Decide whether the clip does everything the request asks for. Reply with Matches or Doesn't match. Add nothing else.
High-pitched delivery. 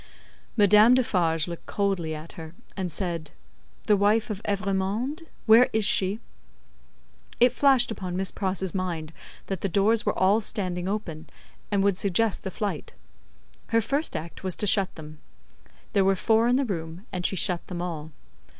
Matches